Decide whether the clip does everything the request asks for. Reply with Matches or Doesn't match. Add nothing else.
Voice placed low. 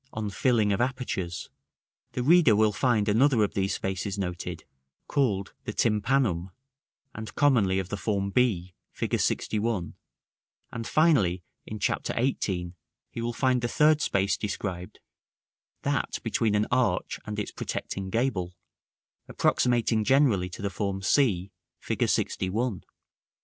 Matches